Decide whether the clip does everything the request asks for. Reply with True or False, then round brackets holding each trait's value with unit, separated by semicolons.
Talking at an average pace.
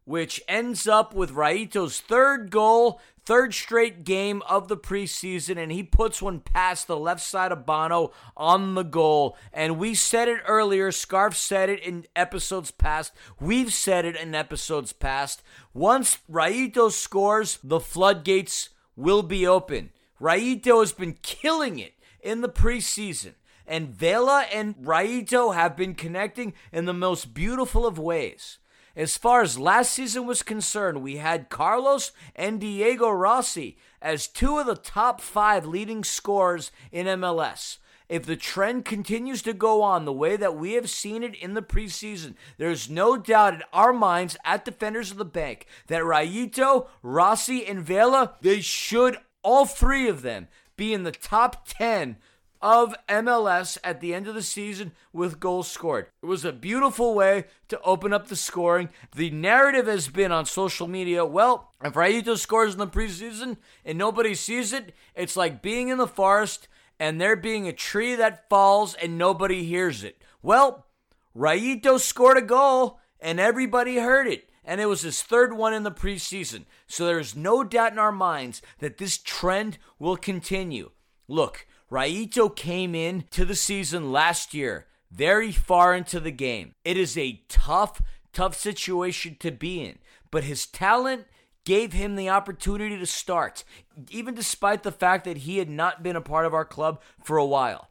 True (170 wpm)